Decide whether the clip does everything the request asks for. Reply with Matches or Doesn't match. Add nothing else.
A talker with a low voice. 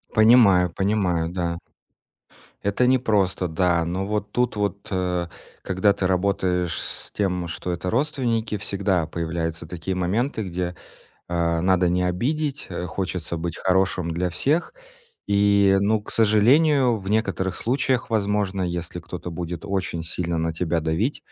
Matches